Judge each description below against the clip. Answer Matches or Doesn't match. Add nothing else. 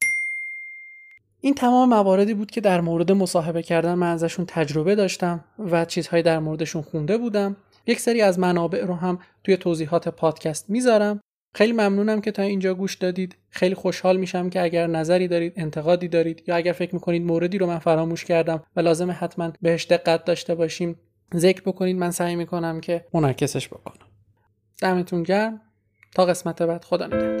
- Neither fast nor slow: Doesn't match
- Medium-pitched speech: Matches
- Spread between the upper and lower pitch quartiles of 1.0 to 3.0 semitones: Matches